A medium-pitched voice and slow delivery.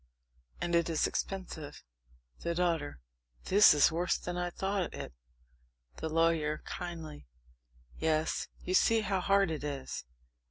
Yes: medium, 170 Hz; slow, 130 wpm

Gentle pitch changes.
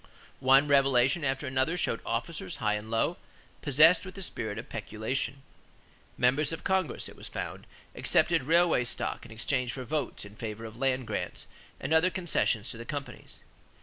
No: wide, 5.5 semitones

